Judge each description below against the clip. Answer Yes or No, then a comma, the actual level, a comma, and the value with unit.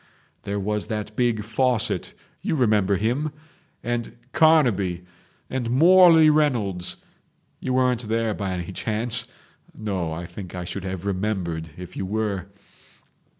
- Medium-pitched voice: No, low, 110 Hz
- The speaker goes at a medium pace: No, slow, 120 wpm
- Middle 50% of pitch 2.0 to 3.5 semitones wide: No, average, 4.9 semitones